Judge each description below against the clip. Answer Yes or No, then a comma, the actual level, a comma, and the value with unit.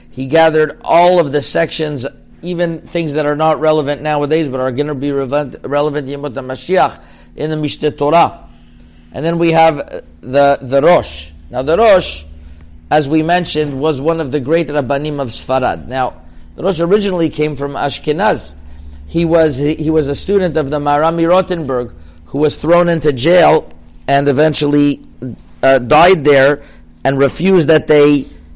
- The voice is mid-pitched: Yes, medium, 145 Hz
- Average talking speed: Yes, average, 165 wpm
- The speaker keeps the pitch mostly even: No, average, 3.4 semitones